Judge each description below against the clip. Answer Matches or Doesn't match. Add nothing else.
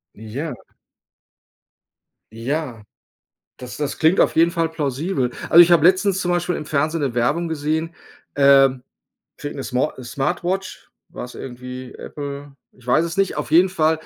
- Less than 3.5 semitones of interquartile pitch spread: Doesn't match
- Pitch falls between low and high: Matches